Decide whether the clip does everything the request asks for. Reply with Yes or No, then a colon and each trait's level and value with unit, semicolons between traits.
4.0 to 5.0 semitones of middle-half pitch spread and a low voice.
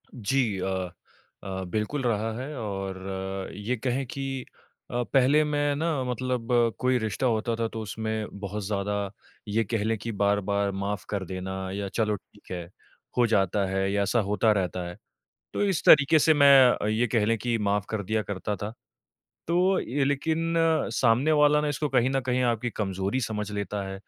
Yes: average, 4.5 semitones; low, 110 Hz